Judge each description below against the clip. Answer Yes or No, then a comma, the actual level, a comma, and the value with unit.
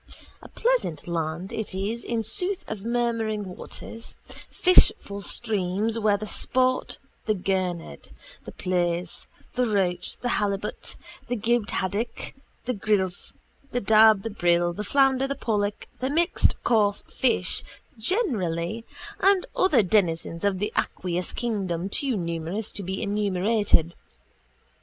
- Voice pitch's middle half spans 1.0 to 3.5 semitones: No, average, 4.2 semitones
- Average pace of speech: No, slow, 125 wpm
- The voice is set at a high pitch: Yes, high, 205 Hz